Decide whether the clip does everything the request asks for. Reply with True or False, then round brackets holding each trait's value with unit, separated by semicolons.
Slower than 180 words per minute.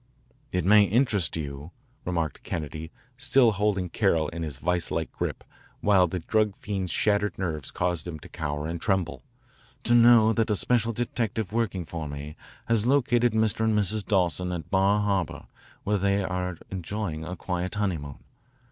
True (165 wpm)